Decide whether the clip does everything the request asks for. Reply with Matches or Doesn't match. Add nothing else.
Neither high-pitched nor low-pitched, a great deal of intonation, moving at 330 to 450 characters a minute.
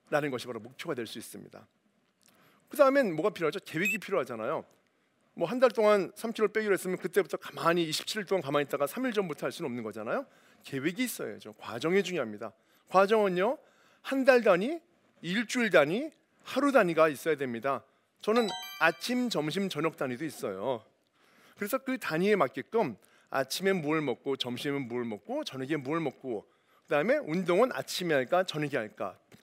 Matches